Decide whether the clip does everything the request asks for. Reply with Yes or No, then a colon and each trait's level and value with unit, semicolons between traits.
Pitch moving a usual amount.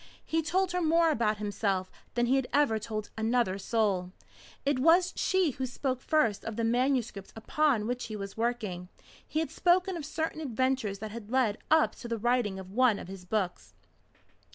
No: wide, 5.8 semitones